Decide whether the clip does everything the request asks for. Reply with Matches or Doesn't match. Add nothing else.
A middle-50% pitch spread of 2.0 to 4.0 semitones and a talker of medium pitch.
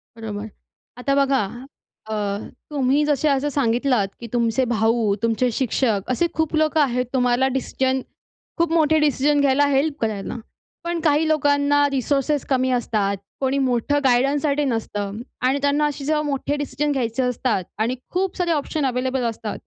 Doesn't match